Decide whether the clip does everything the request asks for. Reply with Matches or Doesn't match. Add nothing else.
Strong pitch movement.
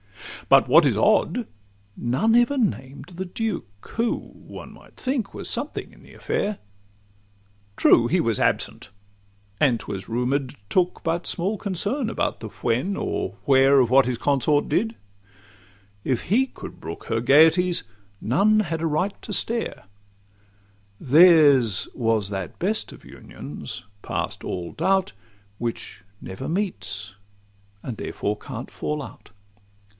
Matches